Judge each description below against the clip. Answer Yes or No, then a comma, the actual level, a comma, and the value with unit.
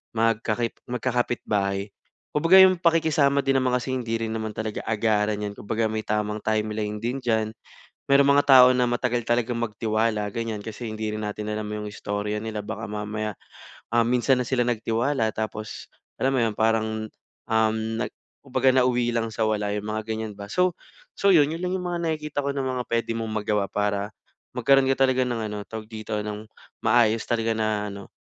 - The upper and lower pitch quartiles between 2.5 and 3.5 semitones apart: Yes, average, 2.8 semitones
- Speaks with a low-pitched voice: Yes, low, 110 Hz